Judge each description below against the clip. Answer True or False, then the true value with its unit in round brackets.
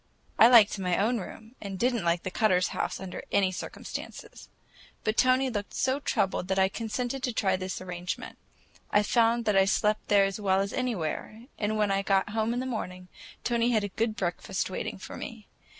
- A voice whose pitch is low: False (205 Hz)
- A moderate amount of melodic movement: True (3.3 semitones)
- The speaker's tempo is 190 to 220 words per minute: True (205 wpm)